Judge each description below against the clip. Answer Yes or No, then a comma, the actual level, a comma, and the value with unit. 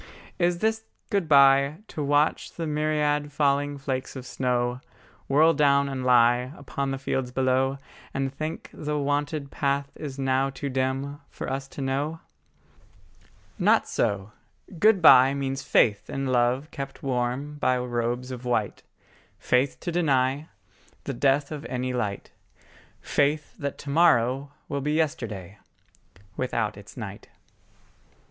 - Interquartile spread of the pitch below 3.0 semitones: Yes, narrow, 2.5 semitones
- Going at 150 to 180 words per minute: No, average, 140 wpm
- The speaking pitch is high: No, low, 135 Hz